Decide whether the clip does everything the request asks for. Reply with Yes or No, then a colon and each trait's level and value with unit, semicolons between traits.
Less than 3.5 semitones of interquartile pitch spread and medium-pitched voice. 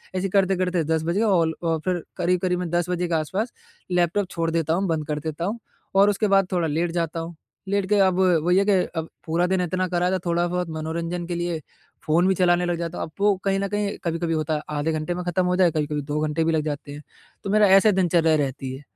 Yes: narrow, 2.4 semitones; medium, 175 Hz